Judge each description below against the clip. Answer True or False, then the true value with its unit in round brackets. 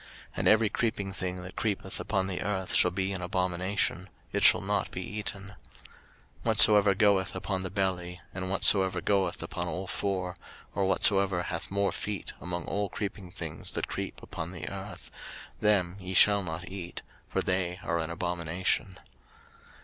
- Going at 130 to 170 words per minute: True (165 wpm)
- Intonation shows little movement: True (1.7 semitones)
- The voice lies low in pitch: True (95 Hz)